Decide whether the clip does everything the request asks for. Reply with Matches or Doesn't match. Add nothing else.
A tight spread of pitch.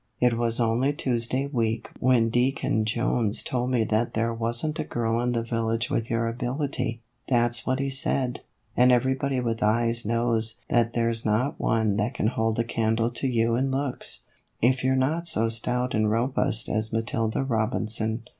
Matches